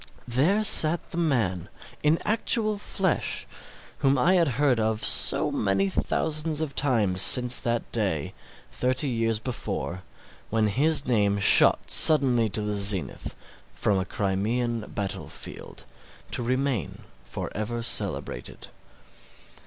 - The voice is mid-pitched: No, low, 120 Hz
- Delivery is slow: Yes, slow, 125 wpm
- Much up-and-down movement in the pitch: Yes, wide, 6.0 semitones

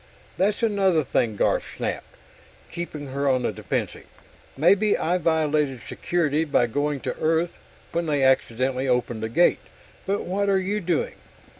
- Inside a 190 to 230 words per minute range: No, average, 150 wpm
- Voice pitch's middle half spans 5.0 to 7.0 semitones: Yes, average, 5.3 semitones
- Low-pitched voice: No, medium, 155 Hz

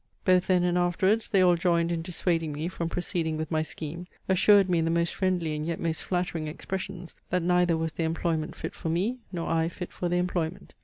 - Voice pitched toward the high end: No, medium, 170 Hz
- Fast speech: Yes, fast, 220 wpm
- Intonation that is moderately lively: No, narrow, 1.8 semitones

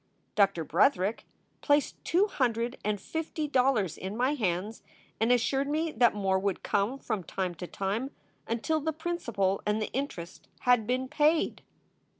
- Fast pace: No, average, 155 wpm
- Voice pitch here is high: Yes, high, 235 Hz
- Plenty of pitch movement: Yes, wide, 6.2 semitones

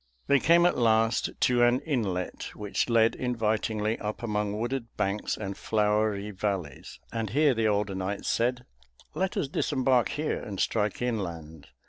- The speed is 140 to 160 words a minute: Yes, average, 150 wpm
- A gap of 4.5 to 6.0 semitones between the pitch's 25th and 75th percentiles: No, average, 3.2 semitones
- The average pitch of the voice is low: Yes, low, 110 Hz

